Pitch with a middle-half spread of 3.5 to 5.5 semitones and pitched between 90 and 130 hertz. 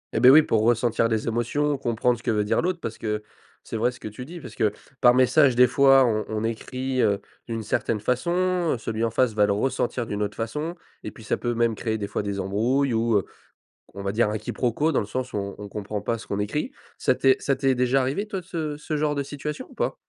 Yes: average, 4.0 semitones; low, 120 Hz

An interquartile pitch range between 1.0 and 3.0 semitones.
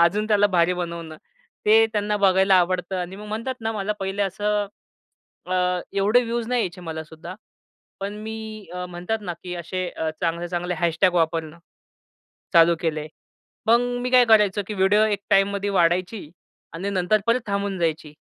No: average, 3.4 semitones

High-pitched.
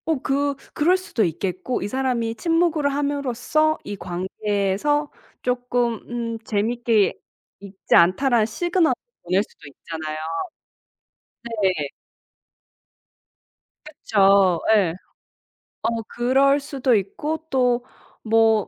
Yes: high, 240 Hz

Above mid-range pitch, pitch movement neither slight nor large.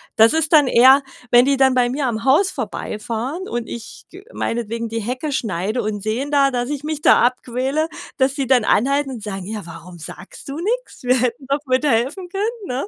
Yes: very high, 255 Hz; average, 4.0 semitones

